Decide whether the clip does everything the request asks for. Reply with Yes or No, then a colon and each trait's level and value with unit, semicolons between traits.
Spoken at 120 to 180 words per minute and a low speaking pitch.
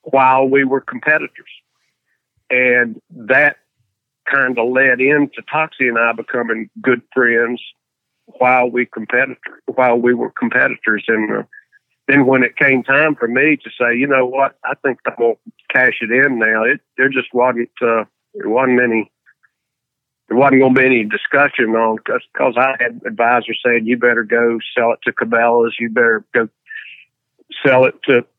Yes: average, 165 wpm; low, 125 Hz